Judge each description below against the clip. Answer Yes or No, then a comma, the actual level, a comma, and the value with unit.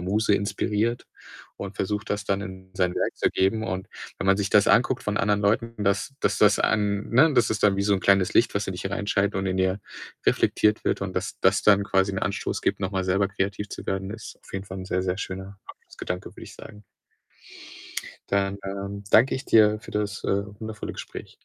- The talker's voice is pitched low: Yes, low, 100 Hz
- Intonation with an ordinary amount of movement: No, narrow, 1.5 semitones